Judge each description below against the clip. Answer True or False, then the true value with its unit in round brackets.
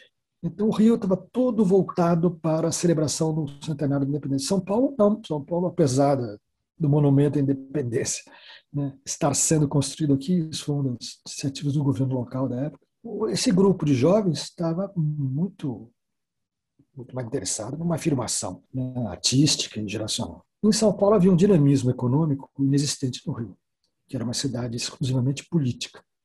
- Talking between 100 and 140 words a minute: False (155 wpm)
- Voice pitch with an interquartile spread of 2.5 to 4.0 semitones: False (4.7 semitones)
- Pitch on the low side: False (145 Hz)